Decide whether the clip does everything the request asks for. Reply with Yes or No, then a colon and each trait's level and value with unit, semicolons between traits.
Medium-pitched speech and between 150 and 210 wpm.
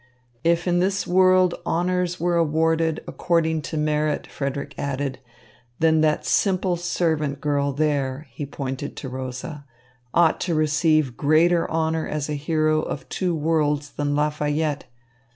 No: medium, 155 Hz; slow, 135 wpm